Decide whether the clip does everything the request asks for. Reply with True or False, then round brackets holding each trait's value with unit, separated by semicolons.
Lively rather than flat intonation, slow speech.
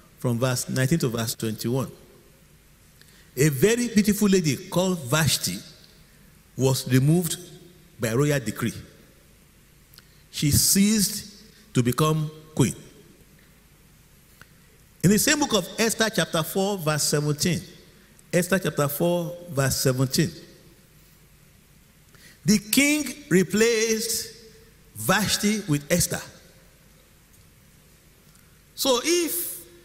True (5.9 semitones; 90 wpm)